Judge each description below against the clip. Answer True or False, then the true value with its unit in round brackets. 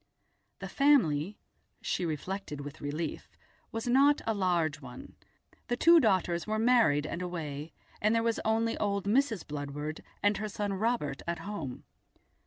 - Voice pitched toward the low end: False (195 Hz)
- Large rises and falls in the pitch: True (6.7 semitones)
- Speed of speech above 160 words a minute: False (145 wpm)